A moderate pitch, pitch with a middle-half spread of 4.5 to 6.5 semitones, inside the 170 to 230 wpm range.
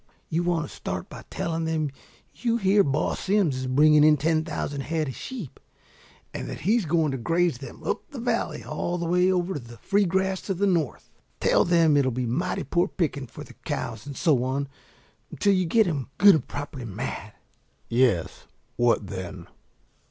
Yes: medium, 155 Hz; average, 5.3 semitones; average, 195 wpm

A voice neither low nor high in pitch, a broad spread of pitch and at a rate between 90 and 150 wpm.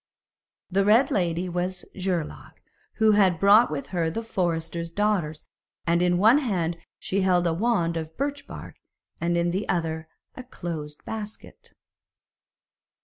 No: medium, 180 Hz; average, 3.8 semitones; average, 145 wpm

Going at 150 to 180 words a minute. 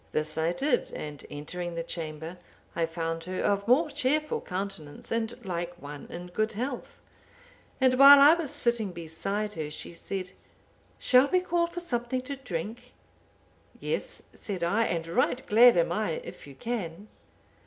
Yes: average, 155 wpm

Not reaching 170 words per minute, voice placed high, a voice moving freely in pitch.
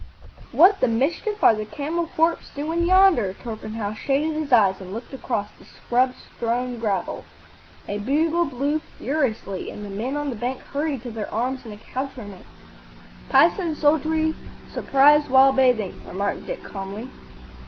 Yes: average, 150 wpm; very high, 260 Hz; wide, 5.9 semitones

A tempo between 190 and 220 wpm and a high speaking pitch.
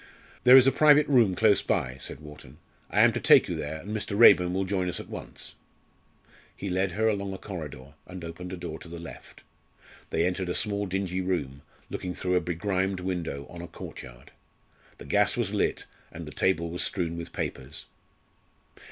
No: average, 195 wpm; very low, 90 Hz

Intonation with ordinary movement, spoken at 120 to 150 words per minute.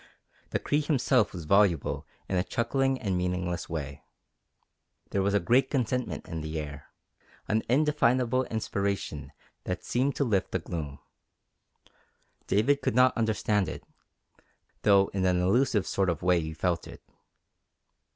No: wide, 6.1 semitones; average, 140 wpm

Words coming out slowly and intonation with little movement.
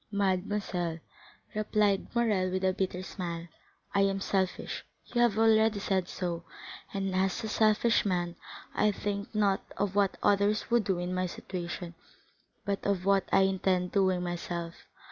No: average, 145 wpm; narrow, 2.2 semitones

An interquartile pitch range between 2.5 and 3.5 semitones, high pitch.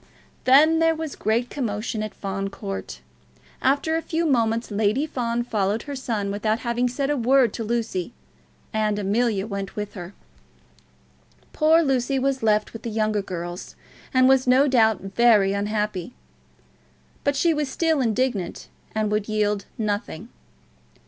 No: average, 4.2 semitones; high, 225 Hz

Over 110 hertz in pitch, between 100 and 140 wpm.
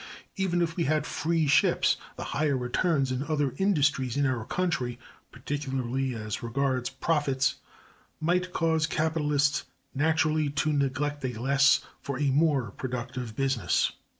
Yes: medium, 140 Hz; slow, 135 wpm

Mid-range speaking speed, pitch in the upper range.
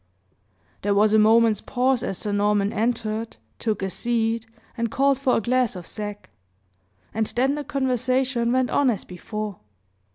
Yes: average, 160 wpm; high, 230 Hz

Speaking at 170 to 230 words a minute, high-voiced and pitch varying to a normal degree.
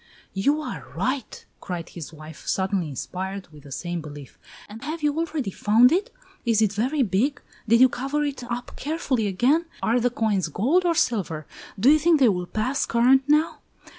No: average, 185 wpm; high, 235 Hz; wide, 7.2 semitones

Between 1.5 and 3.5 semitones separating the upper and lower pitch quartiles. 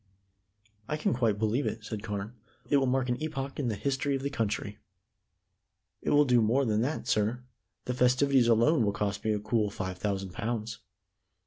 No: average, 4.1 semitones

